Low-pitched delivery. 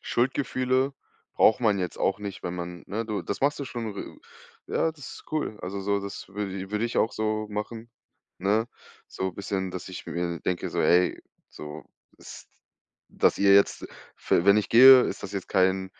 Yes: low, 100 Hz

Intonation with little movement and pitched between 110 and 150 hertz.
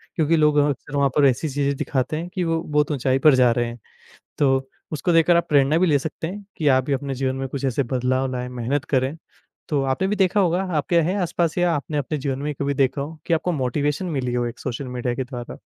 No: average, 3.4 semitones; medium, 140 Hz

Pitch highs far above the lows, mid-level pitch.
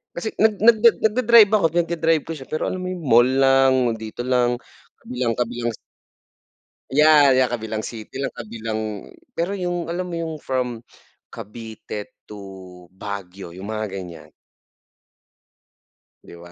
No: wide, 7.5 semitones; low, 125 Hz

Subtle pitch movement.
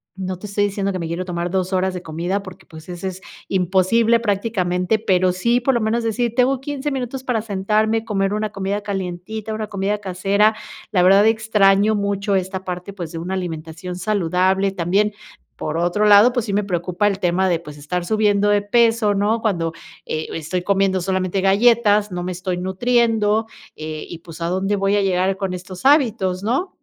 No: average, 3.0 semitones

